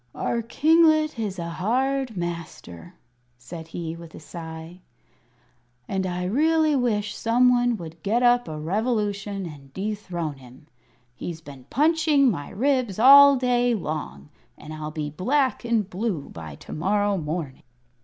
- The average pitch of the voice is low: No, high, 195 Hz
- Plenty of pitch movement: Yes, wide, 7.2 semitones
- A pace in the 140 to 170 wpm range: Yes, average, 145 wpm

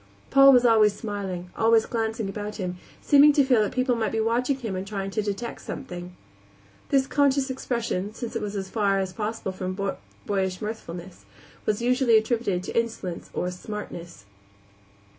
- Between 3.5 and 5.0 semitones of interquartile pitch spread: Yes, average, 3.9 semitones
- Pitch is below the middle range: No, high, 215 Hz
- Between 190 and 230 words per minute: No, average, 165 wpm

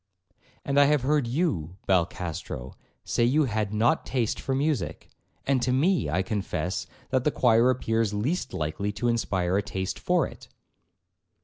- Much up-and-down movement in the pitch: Yes, wide, 5.9 semitones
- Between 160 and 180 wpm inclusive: Yes, average, 165 wpm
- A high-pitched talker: No, low, 115 Hz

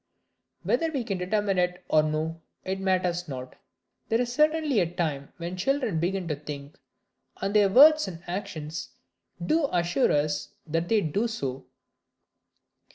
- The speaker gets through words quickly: No, average, 150 wpm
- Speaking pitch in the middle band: Yes, medium, 180 Hz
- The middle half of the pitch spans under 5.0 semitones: No, wide, 5.4 semitones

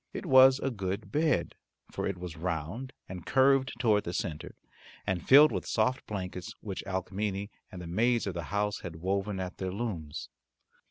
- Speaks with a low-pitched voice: Yes, low, 100 Hz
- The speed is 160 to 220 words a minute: Yes, average, 175 wpm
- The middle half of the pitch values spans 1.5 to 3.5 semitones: No, average, 4.7 semitones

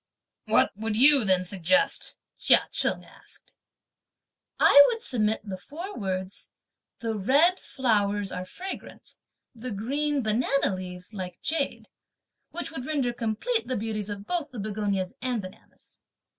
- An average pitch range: No, wide, 5.8 semitones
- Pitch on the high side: Yes, high, 225 Hz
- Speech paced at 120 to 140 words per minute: Yes, slow, 135 wpm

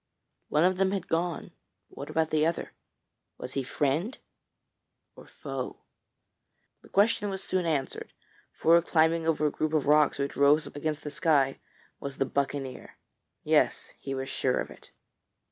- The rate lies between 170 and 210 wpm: No, average, 160 wpm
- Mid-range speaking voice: Yes, medium, 155 Hz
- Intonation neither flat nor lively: Yes, average, 3.2 semitones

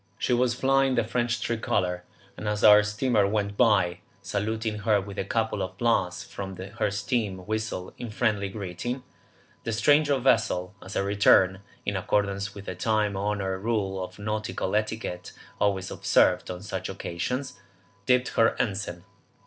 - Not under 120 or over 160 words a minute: Yes, average, 155 wpm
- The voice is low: Yes, low, 105 Hz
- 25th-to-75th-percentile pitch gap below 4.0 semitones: Yes, average, 3.0 semitones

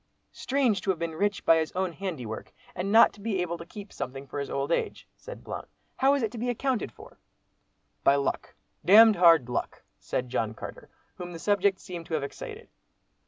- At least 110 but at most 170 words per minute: No, fast, 205 wpm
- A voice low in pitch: No, medium, 180 Hz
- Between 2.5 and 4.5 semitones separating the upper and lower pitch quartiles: No, average, 4.9 semitones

